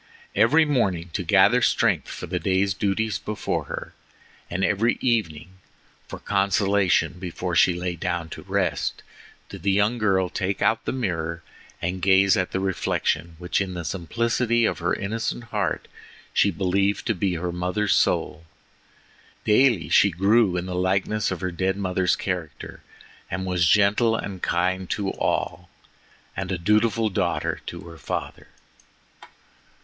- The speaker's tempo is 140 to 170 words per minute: Yes, average, 150 wpm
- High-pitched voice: No, very low, 95 Hz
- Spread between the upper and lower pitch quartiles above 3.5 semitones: No, average, 2.8 semitones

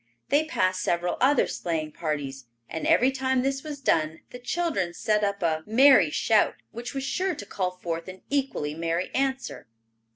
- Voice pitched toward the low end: No, high, 205 Hz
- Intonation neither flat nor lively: No, wide, 8.2 semitones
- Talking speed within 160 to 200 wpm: Yes, average, 170 wpm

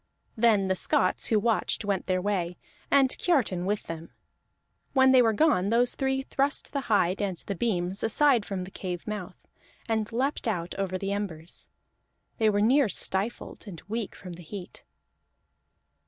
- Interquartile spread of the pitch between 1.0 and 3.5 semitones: No, average, 4.3 semitones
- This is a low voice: No, high, 205 Hz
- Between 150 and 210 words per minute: Yes, average, 165 wpm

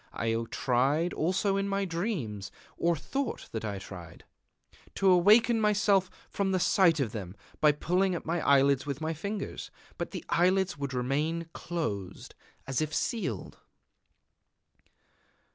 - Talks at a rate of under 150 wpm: Yes, average, 140 wpm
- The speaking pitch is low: No, medium, 165 Hz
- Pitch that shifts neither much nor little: No, wide, 6.4 semitones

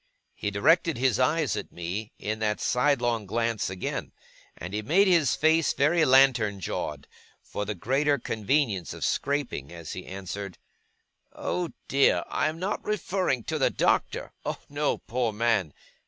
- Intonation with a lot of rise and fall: Yes, wide, 6.2 semitones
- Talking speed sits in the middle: Yes, average, 155 wpm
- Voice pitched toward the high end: No, low, 120 Hz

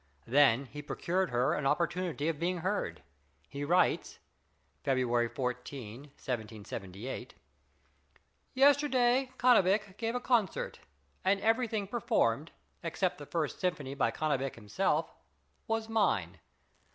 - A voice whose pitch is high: No, medium, 155 Hz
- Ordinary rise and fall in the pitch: No, wide, 8.3 semitones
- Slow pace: Yes, slow, 110 wpm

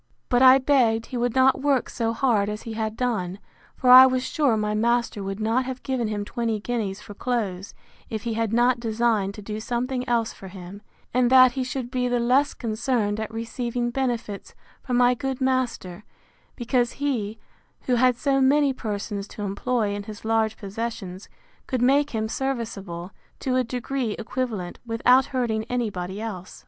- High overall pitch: Yes, high, 235 Hz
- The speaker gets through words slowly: No, average, 180 wpm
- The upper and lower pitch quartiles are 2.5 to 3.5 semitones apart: Yes, average, 3.2 semitones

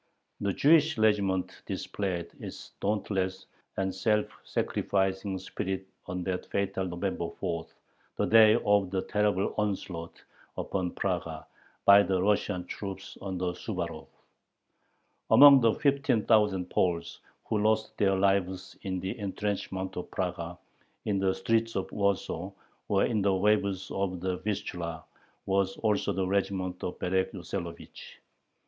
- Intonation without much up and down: Yes, narrow, 1.9 semitones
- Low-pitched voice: Yes, very low, 95 Hz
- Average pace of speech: No, slow, 130 wpm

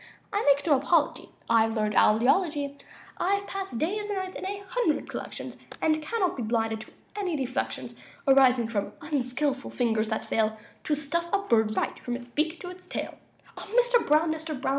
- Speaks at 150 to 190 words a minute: Yes, average, 185 wpm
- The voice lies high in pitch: Yes, very high, 285 Hz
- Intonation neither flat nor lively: No, wide, 7.1 semitones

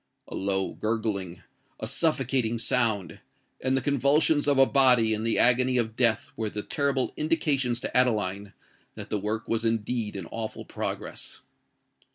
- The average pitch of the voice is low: Yes, low, 115 Hz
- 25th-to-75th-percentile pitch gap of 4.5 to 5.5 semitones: No, average, 3.7 semitones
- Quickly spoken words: No, average, 145 wpm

